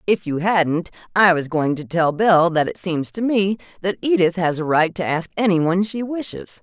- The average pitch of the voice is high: No, medium, 180 Hz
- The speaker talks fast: Yes, fast, 225 wpm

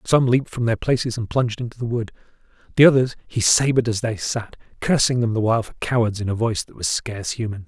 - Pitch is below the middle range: Yes, low, 115 Hz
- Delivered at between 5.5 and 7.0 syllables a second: Yes, 6.3 syllables/s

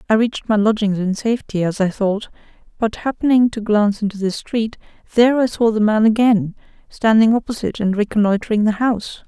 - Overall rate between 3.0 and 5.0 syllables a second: No, 6.0 syllables/s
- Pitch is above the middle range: Yes, high, 215 Hz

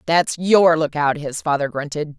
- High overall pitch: No, medium, 155 Hz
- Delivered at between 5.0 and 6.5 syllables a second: No, 4.5 syllables/s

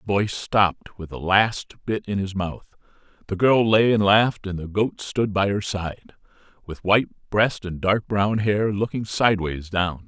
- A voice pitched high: No, low, 100 Hz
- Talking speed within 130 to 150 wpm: No, average, 190 wpm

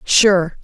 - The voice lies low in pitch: No, medium, 185 Hz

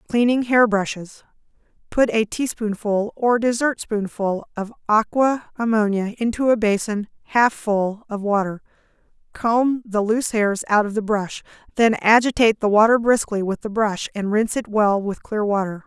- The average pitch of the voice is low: No, high, 215 Hz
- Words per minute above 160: No, average, 150 wpm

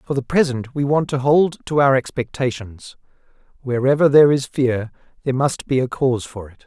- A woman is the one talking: No, male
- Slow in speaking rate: No, average, 190 wpm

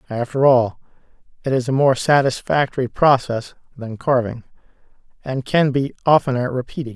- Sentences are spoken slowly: Yes, slow, 130 wpm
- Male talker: Yes, male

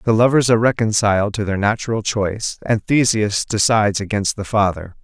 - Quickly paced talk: No, average, 165 wpm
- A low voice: Yes, low, 105 Hz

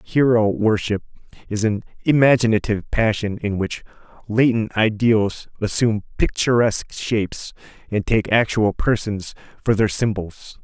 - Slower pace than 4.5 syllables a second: No, 4.6 syllables/s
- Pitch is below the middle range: Yes, low, 110 Hz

